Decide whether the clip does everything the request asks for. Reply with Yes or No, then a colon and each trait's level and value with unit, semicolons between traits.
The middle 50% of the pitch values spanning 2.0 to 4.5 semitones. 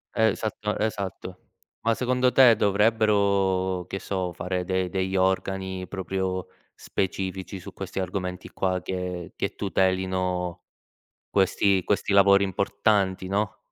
No: narrow, 1.4 semitones